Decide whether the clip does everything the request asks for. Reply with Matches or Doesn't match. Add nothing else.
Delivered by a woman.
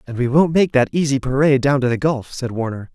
Doesn't match